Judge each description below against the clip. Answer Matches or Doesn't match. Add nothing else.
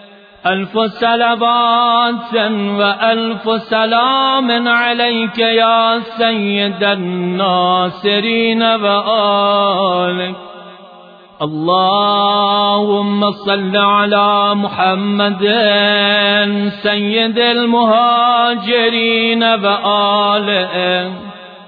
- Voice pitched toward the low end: Doesn't match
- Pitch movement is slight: Matches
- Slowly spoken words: Matches